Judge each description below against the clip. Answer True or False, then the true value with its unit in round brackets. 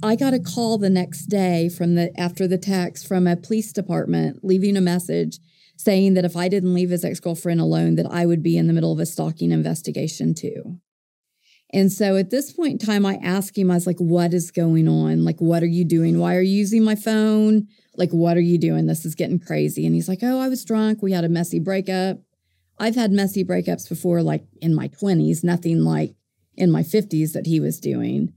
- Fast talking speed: True (230 wpm)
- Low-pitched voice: False (175 Hz)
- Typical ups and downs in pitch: True (3.0 semitones)